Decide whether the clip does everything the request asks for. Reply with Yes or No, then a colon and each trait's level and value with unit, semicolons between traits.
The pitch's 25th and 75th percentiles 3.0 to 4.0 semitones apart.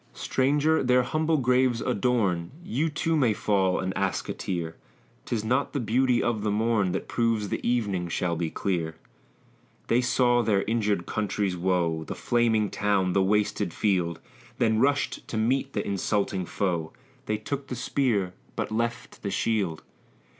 No: average, 4.7 semitones